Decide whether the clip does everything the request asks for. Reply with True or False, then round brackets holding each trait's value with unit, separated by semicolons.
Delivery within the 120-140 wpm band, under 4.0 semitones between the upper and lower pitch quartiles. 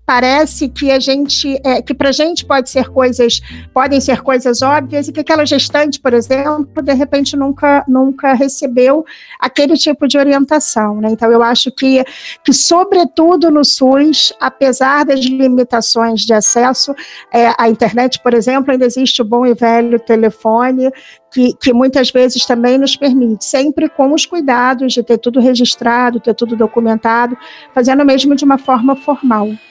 False (165 wpm; 2.6 semitones)